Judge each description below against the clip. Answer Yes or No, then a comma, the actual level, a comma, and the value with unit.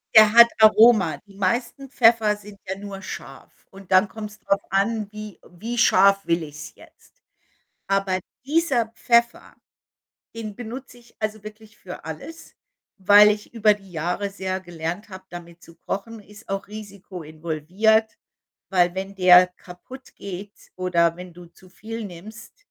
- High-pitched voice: Yes, high, 200 Hz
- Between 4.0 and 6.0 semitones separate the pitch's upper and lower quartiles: No, average, 3.2 semitones